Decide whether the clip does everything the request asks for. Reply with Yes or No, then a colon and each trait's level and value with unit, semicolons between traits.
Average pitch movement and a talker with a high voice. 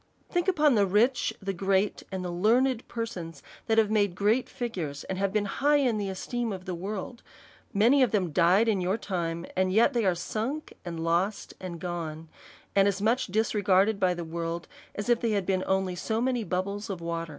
Yes: average, 3.8 semitones; high, 200 Hz